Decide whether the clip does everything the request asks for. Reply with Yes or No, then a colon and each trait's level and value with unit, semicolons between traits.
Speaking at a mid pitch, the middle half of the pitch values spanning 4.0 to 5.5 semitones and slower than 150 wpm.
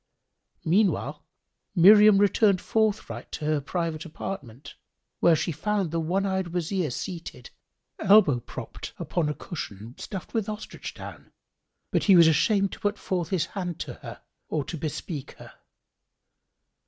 Yes: medium, 175 Hz; average, 4.3 semitones; average, 140 wpm